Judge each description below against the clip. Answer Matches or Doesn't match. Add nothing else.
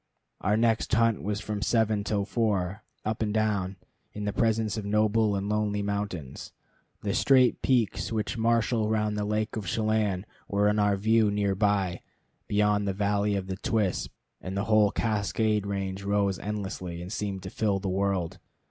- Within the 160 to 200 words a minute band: Matches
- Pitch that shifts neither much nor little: Doesn't match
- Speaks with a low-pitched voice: Matches